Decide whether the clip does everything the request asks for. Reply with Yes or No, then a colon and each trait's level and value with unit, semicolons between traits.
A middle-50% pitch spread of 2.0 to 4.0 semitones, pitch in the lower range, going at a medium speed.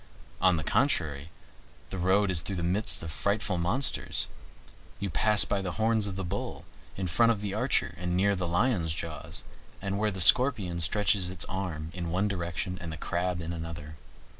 Yes: average, 3.1 semitones; very low, 90 Hz; average, 190 wpm